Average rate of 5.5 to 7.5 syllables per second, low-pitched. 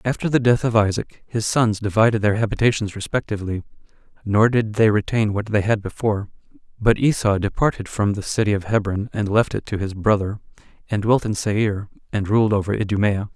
Yes: 5.6 syllables/s; low, 105 Hz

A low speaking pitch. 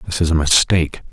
Yes: very low, 80 Hz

